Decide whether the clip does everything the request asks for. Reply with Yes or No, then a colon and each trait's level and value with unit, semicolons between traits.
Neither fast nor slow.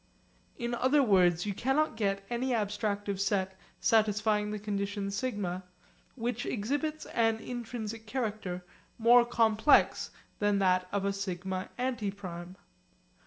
No: slow, 120 wpm